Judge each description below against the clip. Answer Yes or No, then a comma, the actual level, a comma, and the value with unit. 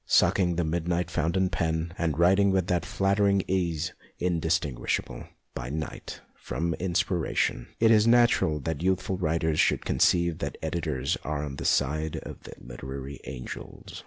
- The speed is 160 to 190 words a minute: No, average, 150 wpm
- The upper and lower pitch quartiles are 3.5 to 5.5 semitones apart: No, average, 3.1 semitones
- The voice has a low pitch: Yes, very low, 85 Hz